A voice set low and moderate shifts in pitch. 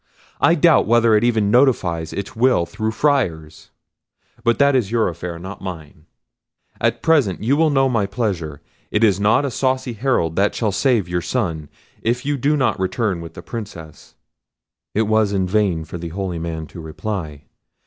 No: low, 100 Hz; wide, 5.9 semitones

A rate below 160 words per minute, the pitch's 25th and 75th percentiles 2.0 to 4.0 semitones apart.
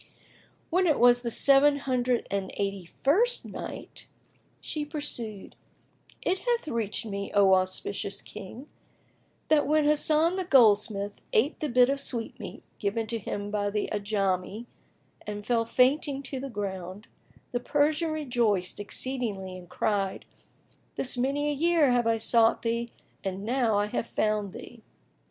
No: average, 145 wpm; wide, 5.5 semitones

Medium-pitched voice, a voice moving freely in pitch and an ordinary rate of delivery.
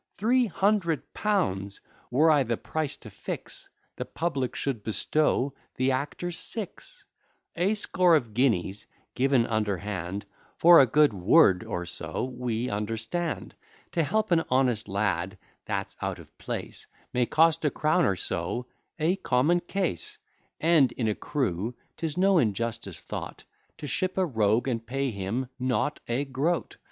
No: low, 130 Hz; wide, 7.1 semitones; average, 145 wpm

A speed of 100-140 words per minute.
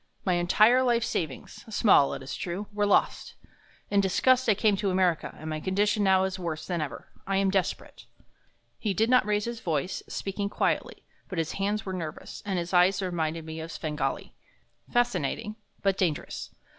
No: average, 180 wpm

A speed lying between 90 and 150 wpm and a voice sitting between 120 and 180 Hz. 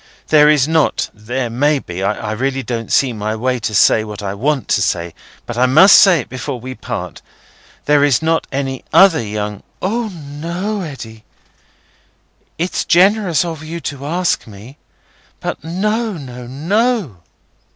Yes: average, 145 wpm; medium, 140 Hz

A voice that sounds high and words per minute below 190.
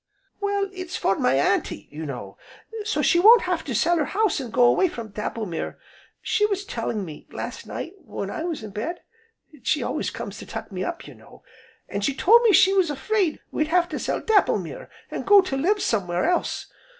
No: very high, 320 Hz; fast, 205 wpm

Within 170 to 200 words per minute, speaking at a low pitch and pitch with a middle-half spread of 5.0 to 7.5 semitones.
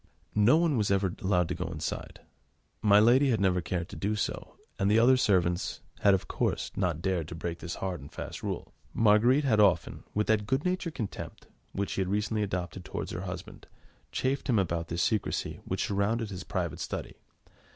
No: average, 195 wpm; low, 100 Hz; average, 3.7 semitones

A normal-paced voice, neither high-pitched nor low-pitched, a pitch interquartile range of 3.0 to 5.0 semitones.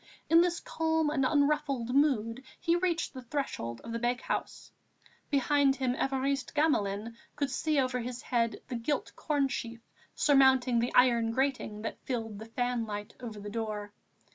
No: average, 150 wpm; very high, 255 Hz; average, 3.8 semitones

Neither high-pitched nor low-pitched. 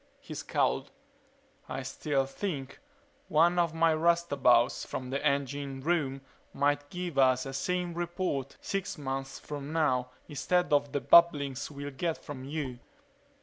Yes: medium, 145 Hz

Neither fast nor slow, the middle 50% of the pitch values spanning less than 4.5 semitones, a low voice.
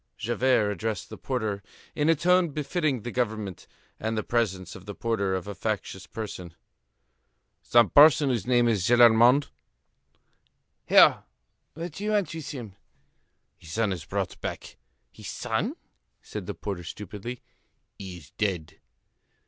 No: average, 145 wpm; average, 4.8 semitones; low, 115 Hz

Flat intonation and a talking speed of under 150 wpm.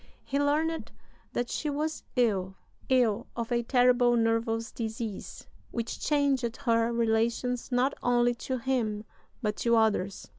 Yes: narrow, 2.2 semitones; slow, 135 wpm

